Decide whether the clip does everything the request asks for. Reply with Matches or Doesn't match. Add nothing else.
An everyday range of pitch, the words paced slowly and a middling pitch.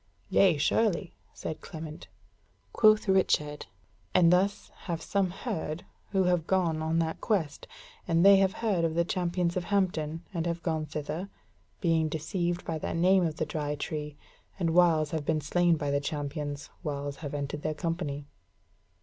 Doesn't match